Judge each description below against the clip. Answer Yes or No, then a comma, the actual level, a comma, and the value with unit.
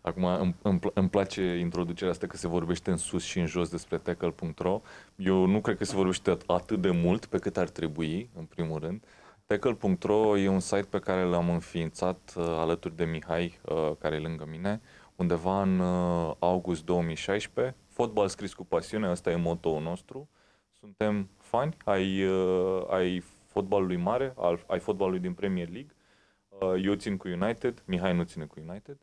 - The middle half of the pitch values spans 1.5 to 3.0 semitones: Yes, narrow, 2.4 semitones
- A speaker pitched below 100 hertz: Yes, very low, 90 Hz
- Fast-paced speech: Yes, fast, 175 wpm